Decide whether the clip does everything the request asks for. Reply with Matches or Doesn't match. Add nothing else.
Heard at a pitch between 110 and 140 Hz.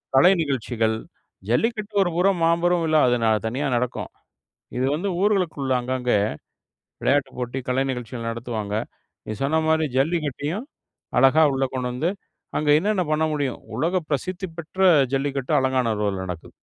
Matches